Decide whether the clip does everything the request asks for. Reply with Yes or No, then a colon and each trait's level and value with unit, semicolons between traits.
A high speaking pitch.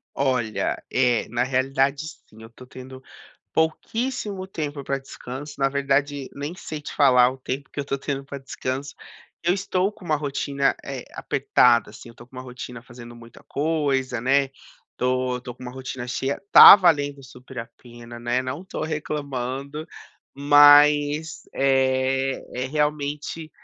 No: low, 135 Hz